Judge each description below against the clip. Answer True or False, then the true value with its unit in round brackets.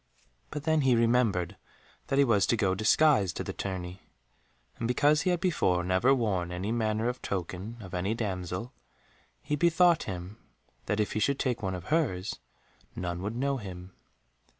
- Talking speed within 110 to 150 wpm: False (175 wpm)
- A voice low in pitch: True (110 Hz)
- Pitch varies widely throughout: True (6.4 semitones)